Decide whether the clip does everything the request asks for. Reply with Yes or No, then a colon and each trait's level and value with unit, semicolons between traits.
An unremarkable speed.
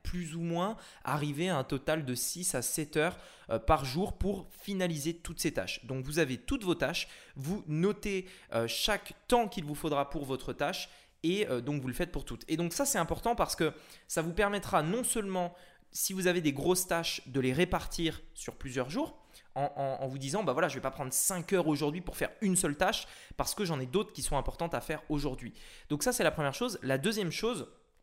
No: fast, 230 wpm